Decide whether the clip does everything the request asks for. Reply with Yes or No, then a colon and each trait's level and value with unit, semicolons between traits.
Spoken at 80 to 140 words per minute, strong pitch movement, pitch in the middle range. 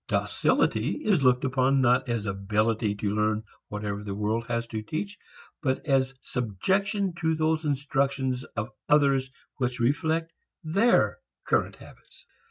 No: slow, 135 wpm; wide, 6.0 semitones; low, 130 Hz